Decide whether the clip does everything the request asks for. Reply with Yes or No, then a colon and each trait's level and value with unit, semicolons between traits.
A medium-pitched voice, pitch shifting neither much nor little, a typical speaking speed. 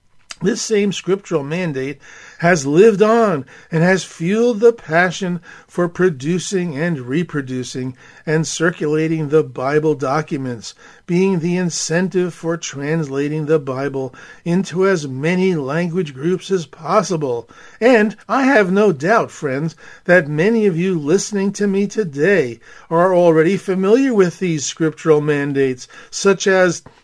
No: medium, 175 Hz; average, 3.8 semitones; slow, 130 wpm